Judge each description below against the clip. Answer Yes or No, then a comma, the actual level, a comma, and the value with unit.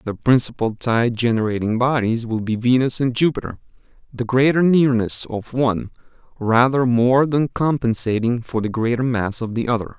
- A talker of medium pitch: No, low, 120 Hz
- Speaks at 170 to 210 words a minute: No, average, 155 wpm